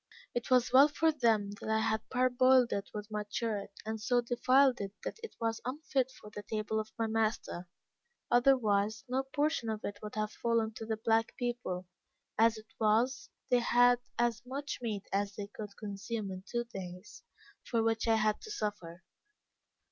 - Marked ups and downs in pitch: No, average, 2.7 semitones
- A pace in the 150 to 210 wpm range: Yes, average, 180 wpm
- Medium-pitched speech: No, high, 225 Hz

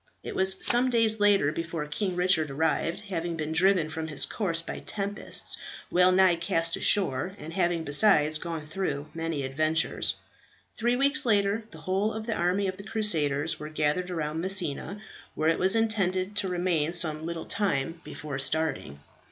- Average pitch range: Yes, average, 4.2 semitones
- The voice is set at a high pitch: No, medium, 170 Hz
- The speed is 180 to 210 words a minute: No, average, 170 wpm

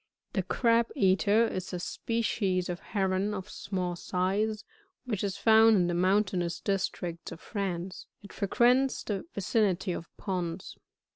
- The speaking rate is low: No, average, 145 wpm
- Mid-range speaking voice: No, high, 195 Hz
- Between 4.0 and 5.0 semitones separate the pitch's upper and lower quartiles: No, average, 2.9 semitones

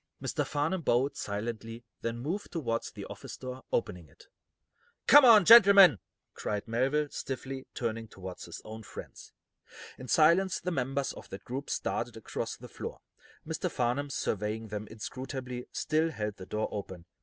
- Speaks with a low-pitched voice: Yes, low, 125 Hz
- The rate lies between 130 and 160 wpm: Yes, average, 155 wpm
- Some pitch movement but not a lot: No, wide, 5.8 semitones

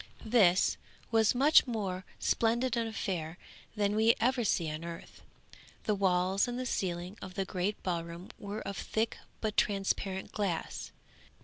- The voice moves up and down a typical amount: Yes, average, 3.7 semitones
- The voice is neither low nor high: No, high, 200 Hz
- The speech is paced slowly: No, average, 145 wpm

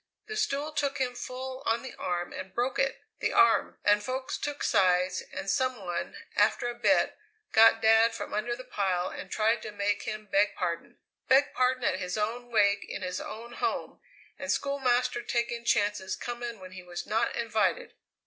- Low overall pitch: No, high, 230 Hz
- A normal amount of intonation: Yes, average, 4.1 semitones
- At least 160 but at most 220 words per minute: Yes, average, 185 wpm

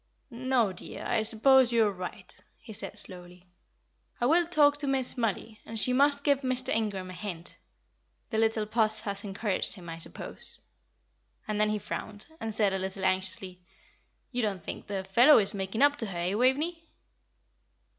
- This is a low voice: No, high, 215 Hz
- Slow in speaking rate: No, average, 175 wpm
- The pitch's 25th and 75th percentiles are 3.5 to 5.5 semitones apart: Yes, average, 4.9 semitones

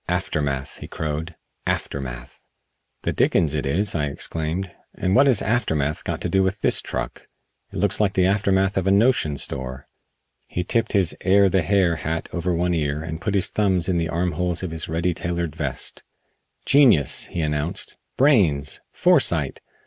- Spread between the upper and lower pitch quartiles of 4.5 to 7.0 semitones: No, average, 4.0 semitones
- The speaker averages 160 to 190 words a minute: Yes, average, 170 wpm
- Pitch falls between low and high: No, very low, 85 Hz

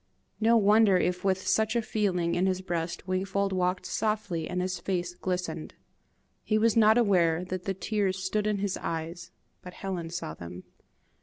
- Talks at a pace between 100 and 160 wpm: No, average, 170 wpm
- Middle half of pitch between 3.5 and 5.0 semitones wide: No, average, 2.7 semitones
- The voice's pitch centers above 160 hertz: Yes, medium, 185 Hz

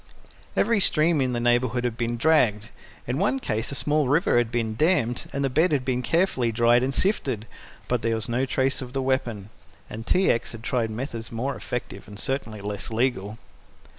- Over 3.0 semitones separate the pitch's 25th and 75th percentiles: Yes, average, 3.4 semitones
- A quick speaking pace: No, average, 195 wpm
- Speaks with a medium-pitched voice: No, low, 125 Hz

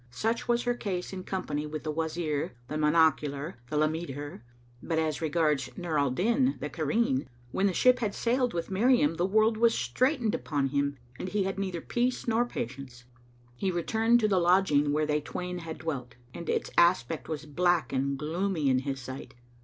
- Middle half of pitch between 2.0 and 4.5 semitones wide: No, average, 5.3 semitones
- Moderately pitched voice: Yes, medium, 165 Hz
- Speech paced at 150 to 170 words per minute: No, average, 185 wpm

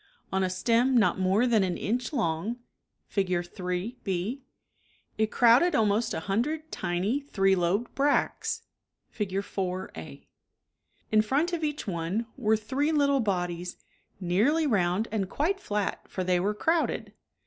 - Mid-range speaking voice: No, high, 210 Hz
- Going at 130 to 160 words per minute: Yes, average, 150 wpm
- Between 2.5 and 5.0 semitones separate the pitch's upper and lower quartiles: No, wide, 5.5 semitones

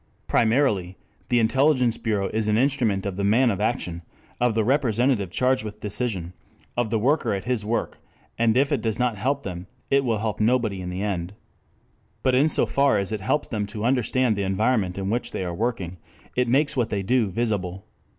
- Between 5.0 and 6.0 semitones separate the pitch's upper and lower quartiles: No, average, 4.1 semitones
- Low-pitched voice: Yes, low, 110 Hz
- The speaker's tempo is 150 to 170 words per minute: No, average, 200 wpm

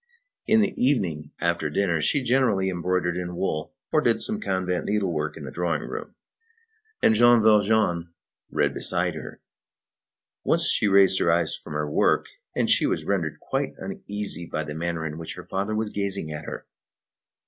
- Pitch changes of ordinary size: Yes, average, 4.2 semitones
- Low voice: Yes, very low, 90 Hz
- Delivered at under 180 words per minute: Yes, average, 170 wpm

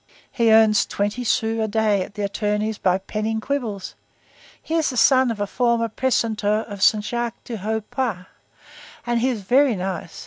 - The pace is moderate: Yes, average, 180 wpm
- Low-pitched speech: No, high, 220 Hz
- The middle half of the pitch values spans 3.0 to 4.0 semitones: No, narrow, 2.6 semitones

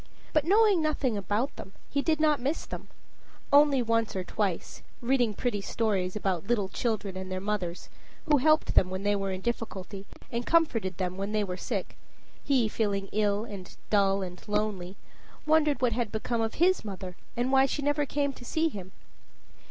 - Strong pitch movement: Yes, wide, 5.9 semitones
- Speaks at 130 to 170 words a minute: No, average, 185 wpm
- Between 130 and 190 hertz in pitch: No, high, 215 Hz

